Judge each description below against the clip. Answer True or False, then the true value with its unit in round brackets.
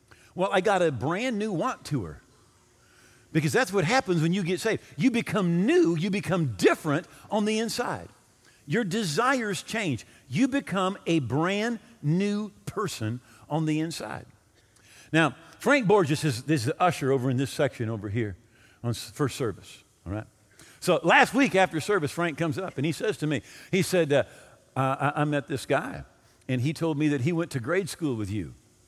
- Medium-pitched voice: True (155 Hz)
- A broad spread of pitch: True (7.2 semitones)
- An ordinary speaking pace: True (185 wpm)